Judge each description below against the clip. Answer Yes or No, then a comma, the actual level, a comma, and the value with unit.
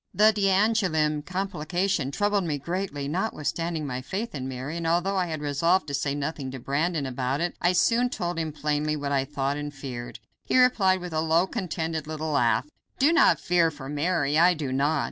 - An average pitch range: Yes, average, 4.3 semitones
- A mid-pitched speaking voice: Yes, medium, 160 Hz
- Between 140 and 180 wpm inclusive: No, average, 195 wpm